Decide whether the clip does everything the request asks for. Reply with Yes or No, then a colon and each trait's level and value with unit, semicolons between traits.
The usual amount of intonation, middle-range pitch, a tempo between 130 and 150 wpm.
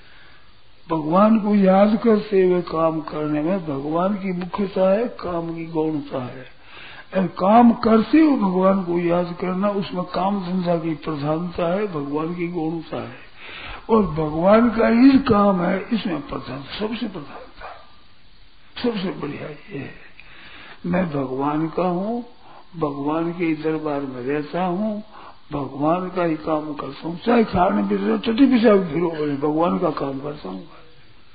Yes: average, 4.8 semitones; medium, 175 Hz; average, 140 wpm